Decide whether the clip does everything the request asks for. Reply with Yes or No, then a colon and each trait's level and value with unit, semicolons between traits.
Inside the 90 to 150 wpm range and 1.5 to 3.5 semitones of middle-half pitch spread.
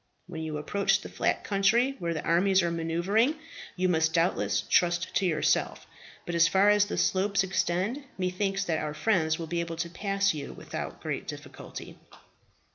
No: average, 175 wpm; average, 3.1 semitones